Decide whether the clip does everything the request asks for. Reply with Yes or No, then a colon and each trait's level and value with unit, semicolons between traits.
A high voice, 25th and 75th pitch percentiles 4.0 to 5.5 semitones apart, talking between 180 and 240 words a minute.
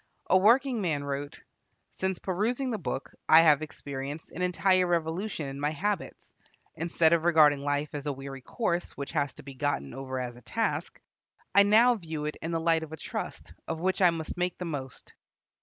No: medium, 160 Hz; average, 4.4 semitones; average, 195 wpm